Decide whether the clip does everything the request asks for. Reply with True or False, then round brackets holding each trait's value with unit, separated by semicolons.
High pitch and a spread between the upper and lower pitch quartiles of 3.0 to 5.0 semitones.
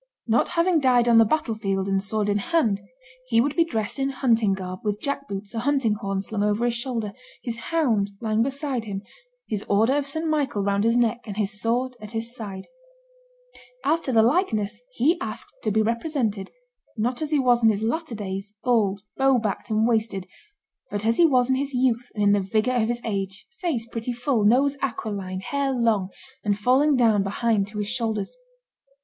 True (230 Hz; 3.9 semitones)